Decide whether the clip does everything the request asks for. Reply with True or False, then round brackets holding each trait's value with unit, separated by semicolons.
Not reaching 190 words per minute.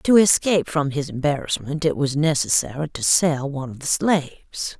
True (175 wpm)